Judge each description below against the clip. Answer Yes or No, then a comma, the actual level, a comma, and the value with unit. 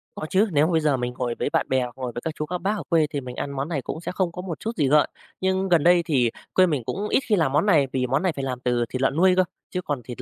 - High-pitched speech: No, medium, 150 Hz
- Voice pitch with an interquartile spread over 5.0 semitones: Yes, wide, 5.5 semitones